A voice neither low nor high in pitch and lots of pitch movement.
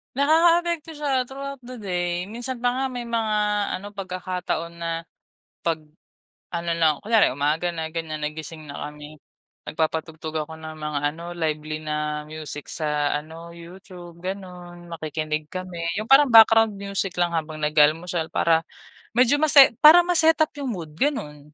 Yes: medium, 170 Hz; wide, 6.6 semitones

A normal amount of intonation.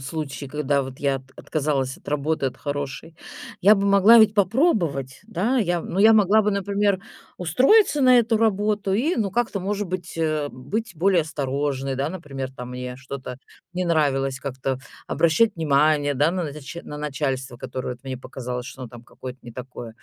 No: wide, 6.7 semitones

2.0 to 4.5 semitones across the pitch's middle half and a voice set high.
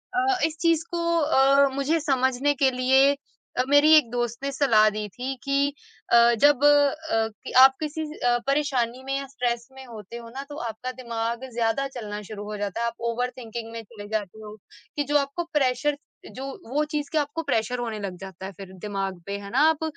Yes: average, 4.0 semitones; very high, 255 Hz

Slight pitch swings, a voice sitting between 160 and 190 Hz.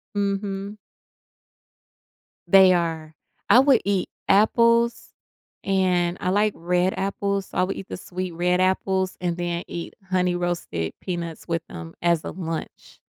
Yes: narrow, 2.2 semitones; medium, 185 Hz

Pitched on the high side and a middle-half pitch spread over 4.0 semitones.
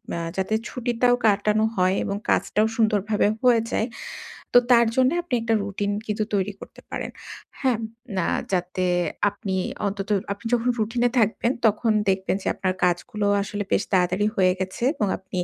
No: high, 210 Hz; average, 3.3 semitones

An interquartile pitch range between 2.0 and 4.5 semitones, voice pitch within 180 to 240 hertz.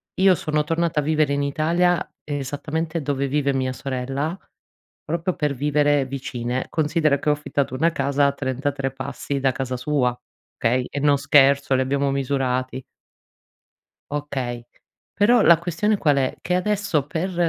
No: average, 2.9 semitones; medium, 145 Hz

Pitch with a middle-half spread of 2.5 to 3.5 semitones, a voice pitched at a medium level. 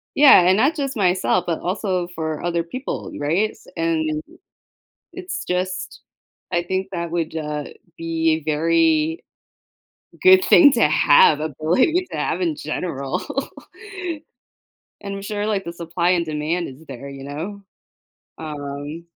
No: average, 3.9 semitones; medium, 170 Hz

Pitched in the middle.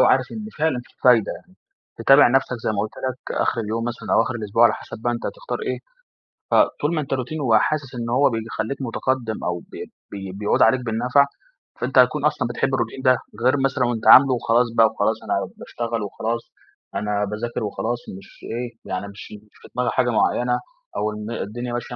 No: low, 120 Hz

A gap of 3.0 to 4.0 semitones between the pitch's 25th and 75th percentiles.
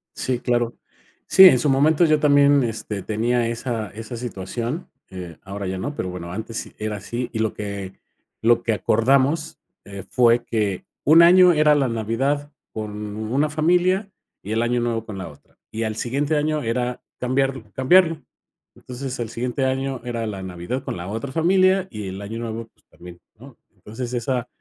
No: average, 4.6 semitones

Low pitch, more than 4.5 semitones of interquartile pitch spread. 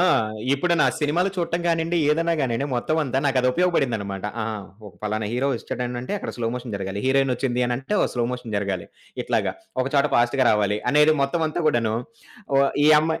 Yes: low, 130 Hz; average, 5.2 semitones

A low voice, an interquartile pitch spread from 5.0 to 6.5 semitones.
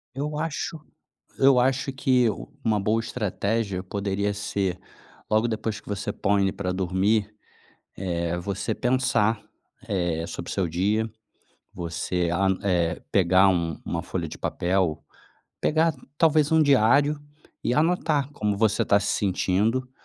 Yes: low, 105 Hz; average, 5.3 semitones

